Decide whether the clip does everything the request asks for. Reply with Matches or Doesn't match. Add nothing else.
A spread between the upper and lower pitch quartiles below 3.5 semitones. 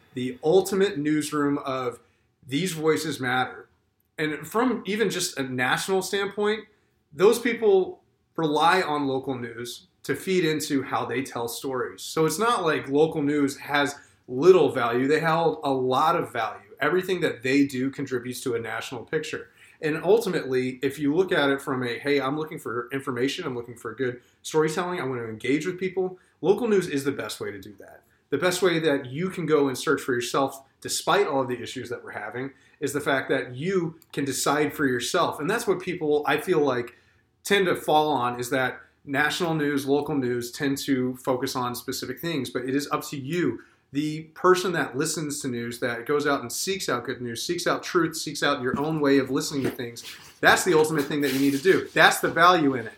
Doesn't match